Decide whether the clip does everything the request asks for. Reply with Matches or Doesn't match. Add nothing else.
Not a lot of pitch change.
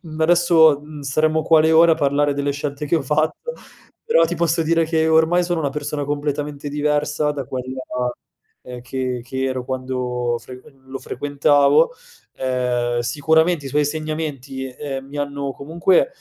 Doesn't match